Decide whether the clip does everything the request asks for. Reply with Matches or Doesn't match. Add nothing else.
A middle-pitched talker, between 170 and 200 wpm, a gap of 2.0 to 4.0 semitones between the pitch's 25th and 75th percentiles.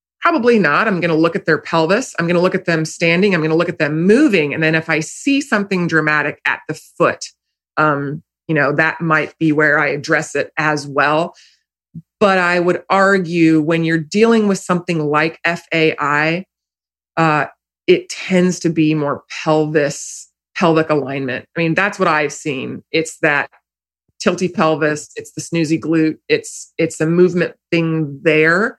Matches